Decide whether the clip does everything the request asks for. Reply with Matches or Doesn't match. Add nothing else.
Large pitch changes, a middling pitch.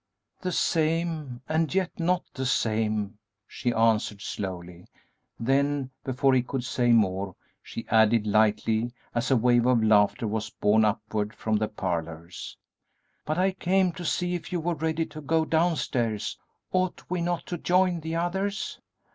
Doesn't match